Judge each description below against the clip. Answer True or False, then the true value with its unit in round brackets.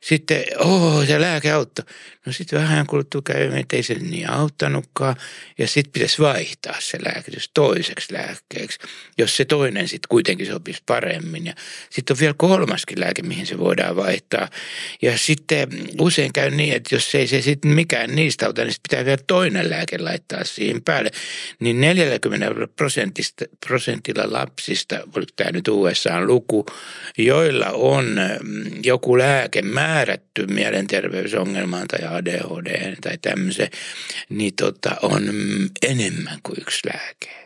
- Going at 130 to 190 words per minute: True (145 wpm)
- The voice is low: False (150 Hz)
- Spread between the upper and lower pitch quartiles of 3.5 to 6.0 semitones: True (4.5 semitones)